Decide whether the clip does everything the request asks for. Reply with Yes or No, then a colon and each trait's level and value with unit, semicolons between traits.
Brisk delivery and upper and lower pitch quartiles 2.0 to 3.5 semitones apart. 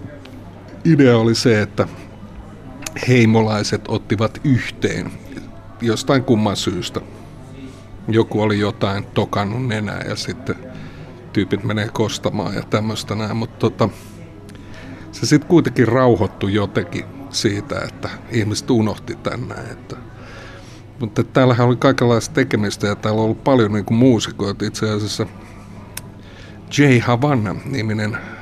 No: average, 110 wpm; average, 3.2 semitones